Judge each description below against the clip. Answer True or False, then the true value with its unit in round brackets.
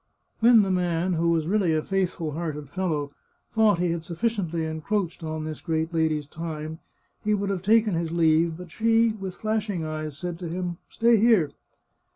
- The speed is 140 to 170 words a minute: False (185 wpm)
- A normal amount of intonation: True (4.0 semitones)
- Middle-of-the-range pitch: True (170 Hz)